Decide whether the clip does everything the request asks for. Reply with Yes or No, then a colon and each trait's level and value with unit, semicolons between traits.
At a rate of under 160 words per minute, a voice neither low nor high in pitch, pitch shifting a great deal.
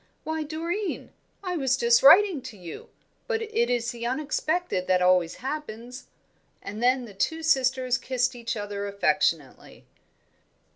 No: average, 140 wpm; very high, 250 Hz; wide, 7.1 semitones